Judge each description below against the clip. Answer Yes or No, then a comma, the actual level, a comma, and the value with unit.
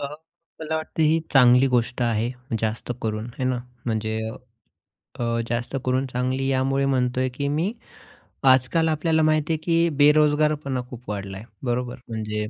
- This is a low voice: Yes, low, 130 Hz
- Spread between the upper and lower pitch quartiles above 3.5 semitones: Yes, average, 4.1 semitones